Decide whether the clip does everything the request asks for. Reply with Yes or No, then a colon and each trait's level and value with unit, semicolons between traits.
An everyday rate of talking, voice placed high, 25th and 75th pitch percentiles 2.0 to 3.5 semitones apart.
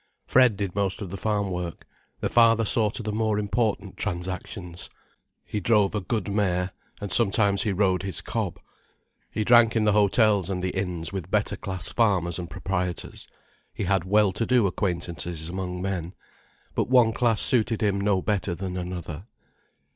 No: average, 170 wpm; low, 100 Hz; average, 2.9 semitones